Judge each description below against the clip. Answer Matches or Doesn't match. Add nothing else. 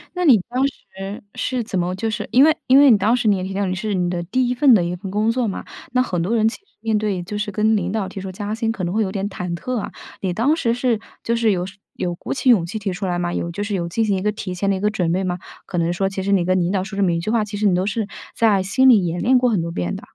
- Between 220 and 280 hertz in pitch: Doesn't match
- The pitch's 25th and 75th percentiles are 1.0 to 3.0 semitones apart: Doesn't match